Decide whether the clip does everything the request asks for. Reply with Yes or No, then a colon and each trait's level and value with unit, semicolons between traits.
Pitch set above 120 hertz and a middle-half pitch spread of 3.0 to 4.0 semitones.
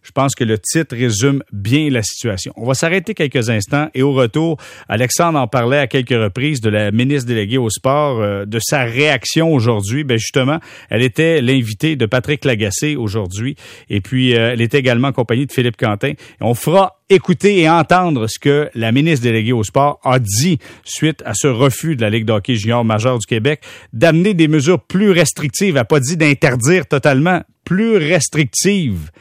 No: low, 135 Hz; average, 4.9 semitones